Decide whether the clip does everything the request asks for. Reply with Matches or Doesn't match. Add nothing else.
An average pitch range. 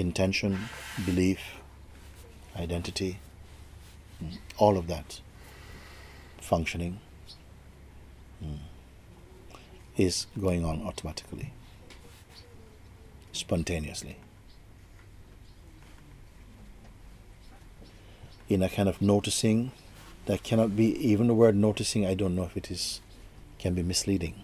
Matches